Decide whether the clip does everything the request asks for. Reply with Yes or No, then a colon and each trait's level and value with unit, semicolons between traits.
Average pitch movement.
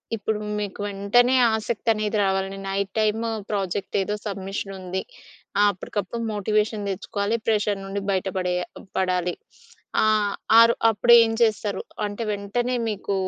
No: narrow, 1.9 semitones